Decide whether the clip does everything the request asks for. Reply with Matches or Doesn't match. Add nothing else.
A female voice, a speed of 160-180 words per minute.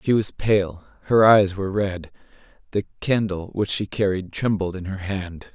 Doesn't match